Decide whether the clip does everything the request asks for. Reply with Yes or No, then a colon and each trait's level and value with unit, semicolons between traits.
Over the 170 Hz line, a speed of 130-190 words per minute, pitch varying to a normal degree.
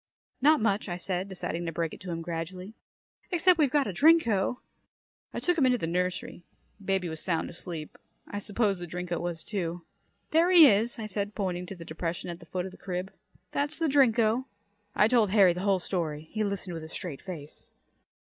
No: high, 190 Hz; fast, 205 wpm; average, 4.5 semitones